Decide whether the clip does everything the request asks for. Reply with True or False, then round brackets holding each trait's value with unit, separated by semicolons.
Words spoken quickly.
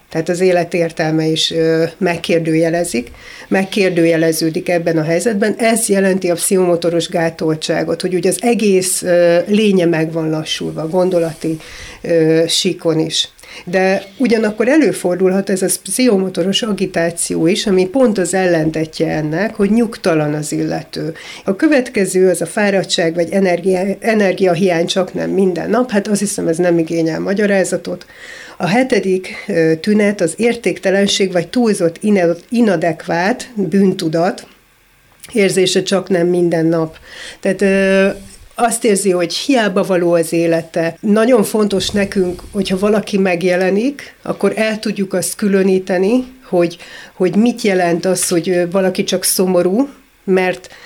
False (130 wpm)